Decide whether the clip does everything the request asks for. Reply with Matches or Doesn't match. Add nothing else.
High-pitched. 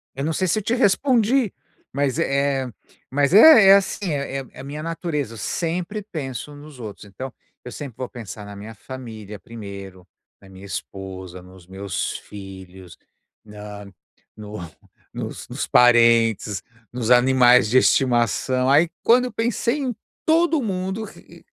Doesn't match